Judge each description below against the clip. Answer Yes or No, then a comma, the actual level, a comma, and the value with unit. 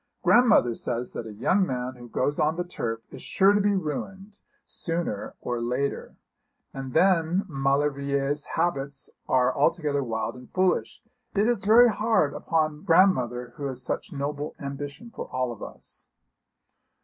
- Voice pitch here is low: No, medium, 145 Hz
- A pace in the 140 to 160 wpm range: Yes, average, 150 wpm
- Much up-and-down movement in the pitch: Yes, wide, 6.3 semitones